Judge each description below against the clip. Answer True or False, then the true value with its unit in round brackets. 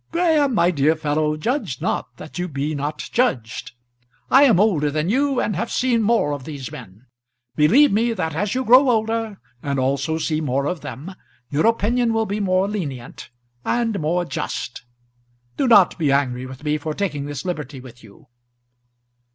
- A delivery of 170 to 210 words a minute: True (175 wpm)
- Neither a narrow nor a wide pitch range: False (7.7 semitones)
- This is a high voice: False (165 Hz)